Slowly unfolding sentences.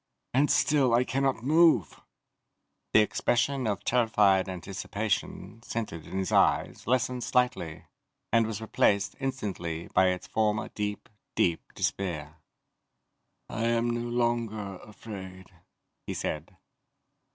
Yes: slow, 115 wpm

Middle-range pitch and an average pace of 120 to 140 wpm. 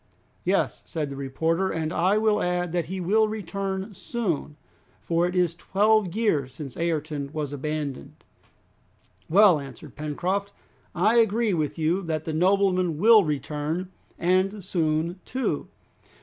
Yes: medium, 175 Hz; slow, 135 wpm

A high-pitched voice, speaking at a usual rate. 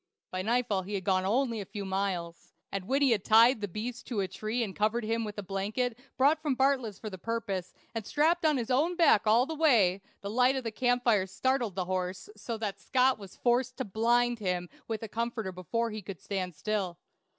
No: high, 220 Hz; fast, 225 wpm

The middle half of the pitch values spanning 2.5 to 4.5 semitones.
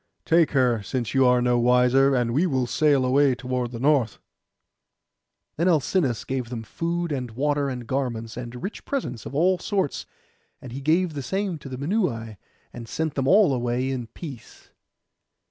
Yes: average, 3.9 semitones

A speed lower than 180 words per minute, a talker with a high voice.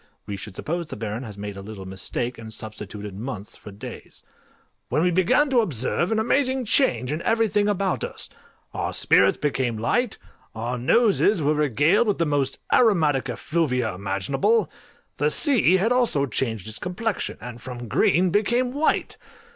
No: average, 165 wpm; medium, 145 Hz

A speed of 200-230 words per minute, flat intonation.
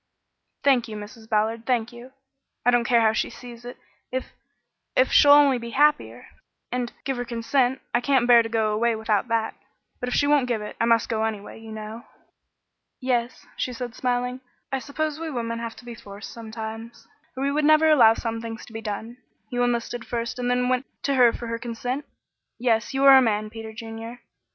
Yes: fast, 205 wpm; narrow, 2.0 semitones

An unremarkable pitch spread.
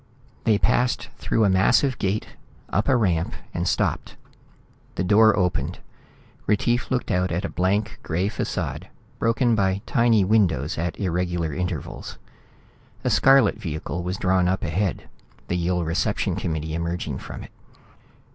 Yes: average, 3.8 semitones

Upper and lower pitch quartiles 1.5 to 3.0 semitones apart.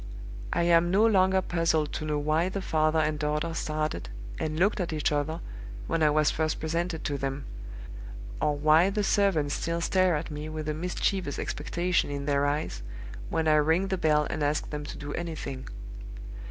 Yes: narrow, 2.4 semitones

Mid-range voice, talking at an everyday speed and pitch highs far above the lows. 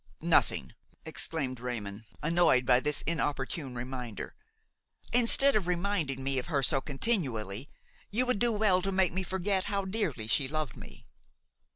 Yes: medium, 155 Hz; average, 150 wpm; wide, 6.9 semitones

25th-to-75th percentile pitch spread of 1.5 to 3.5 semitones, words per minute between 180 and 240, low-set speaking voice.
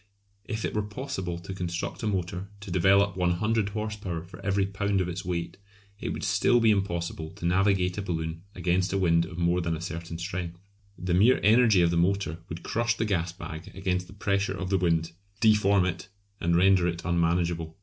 Yes: average, 2.7 semitones; average, 200 wpm; very low, 90 Hz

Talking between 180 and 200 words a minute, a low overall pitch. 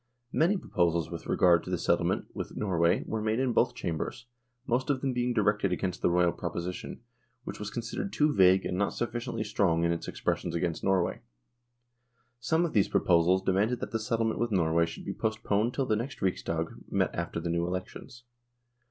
Yes: average, 185 wpm; low, 100 Hz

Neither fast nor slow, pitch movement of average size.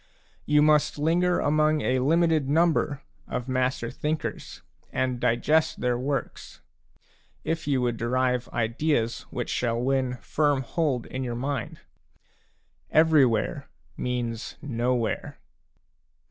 No: slow, 115 wpm; average, 3.7 semitones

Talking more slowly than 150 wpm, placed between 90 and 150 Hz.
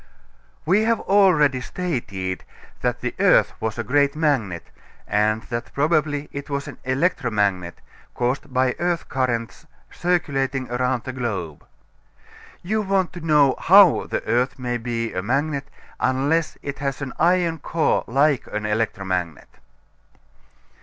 Yes: slow, 135 wpm; low, 135 Hz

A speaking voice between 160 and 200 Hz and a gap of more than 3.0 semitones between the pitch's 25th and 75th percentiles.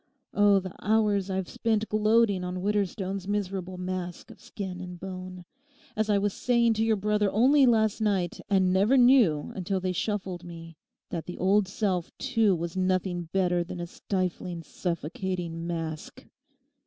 No: high, 190 Hz; average, 2.7 semitones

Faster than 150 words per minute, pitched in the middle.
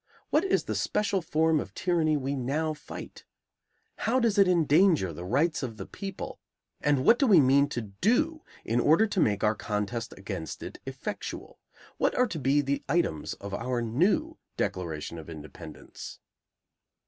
Yes: average, 165 wpm; medium, 145 Hz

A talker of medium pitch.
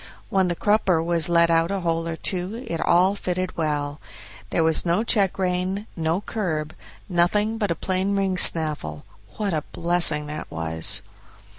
Yes: medium, 175 Hz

